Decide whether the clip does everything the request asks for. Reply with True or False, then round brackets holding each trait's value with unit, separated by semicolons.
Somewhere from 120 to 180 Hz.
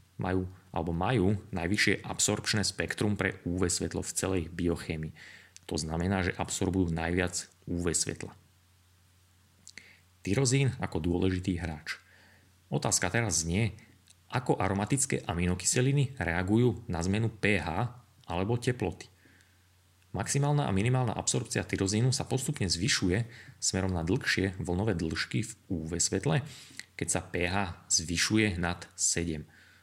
False (95 Hz)